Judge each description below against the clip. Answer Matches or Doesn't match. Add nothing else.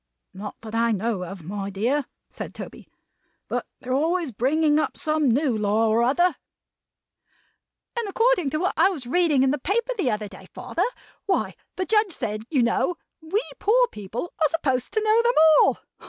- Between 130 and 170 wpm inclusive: Doesn't match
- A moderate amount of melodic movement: Doesn't match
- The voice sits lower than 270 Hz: Doesn't match